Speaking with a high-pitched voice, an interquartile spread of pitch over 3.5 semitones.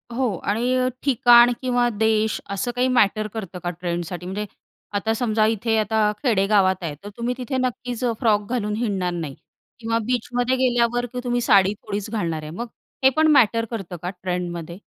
Yes: high, 220 Hz; average, 4.1 semitones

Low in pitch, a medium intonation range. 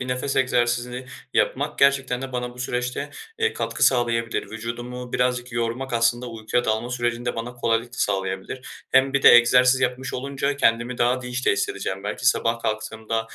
No: low, 125 Hz; narrow, 1.6 semitones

